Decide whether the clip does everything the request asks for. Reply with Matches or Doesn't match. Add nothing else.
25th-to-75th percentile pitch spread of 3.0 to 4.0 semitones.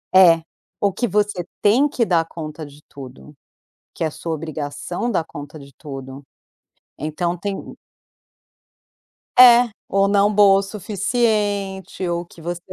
Doesn't match